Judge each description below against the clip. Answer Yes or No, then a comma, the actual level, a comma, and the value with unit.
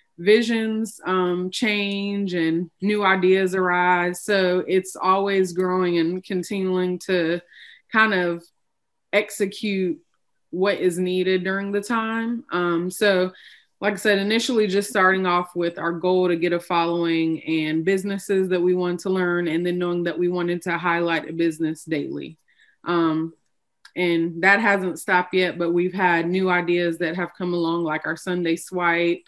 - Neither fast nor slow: Yes, average, 155 wpm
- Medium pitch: Yes, medium, 180 Hz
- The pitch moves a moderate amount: No, narrow, 2.1 semitones